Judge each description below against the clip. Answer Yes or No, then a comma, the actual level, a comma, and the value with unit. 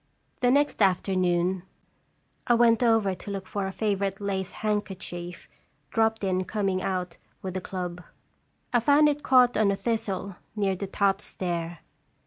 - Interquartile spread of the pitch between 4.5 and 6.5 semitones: No, average, 3.1 semitones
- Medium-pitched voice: No, high, 195 Hz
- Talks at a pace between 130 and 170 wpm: Yes, average, 150 wpm